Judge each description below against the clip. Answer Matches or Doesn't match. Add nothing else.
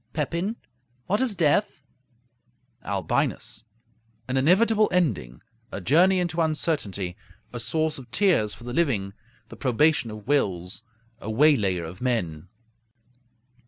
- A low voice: Matches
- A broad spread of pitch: Matches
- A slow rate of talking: Matches